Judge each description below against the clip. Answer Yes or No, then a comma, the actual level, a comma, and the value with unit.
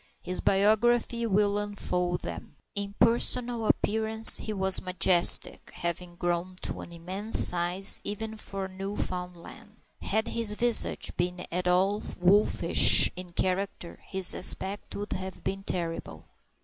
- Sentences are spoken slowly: Yes, slow, 130 wpm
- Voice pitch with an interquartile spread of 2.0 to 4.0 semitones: Yes, average, 2.7 semitones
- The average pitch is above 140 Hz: Yes, high, 190 Hz